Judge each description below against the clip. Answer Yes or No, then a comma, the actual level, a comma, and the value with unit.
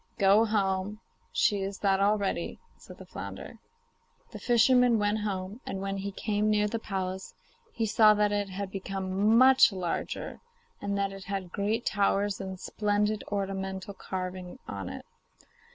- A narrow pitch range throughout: Yes, narrow, 1.6 semitones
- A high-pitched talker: Yes, high, 200 Hz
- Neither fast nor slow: Yes, average, 150 wpm